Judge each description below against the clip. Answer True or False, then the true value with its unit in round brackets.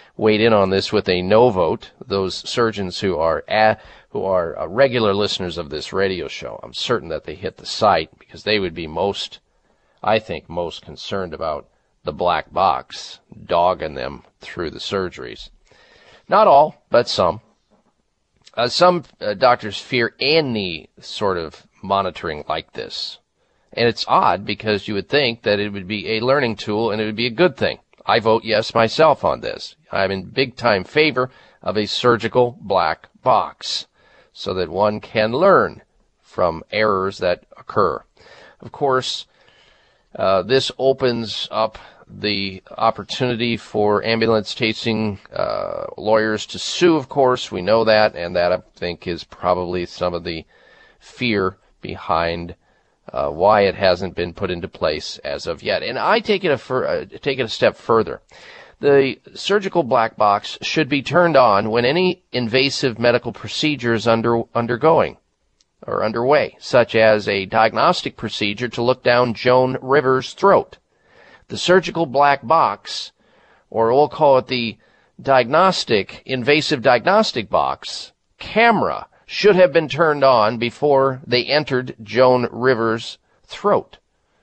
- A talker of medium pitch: False (115 Hz)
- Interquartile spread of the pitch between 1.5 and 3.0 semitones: False (4.3 semitones)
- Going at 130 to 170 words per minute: True (155 wpm)